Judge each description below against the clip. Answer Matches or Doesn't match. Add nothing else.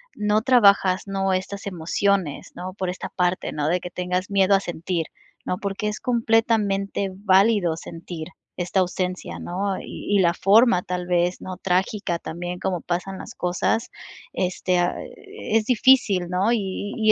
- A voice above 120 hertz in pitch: Matches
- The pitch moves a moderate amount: Doesn't match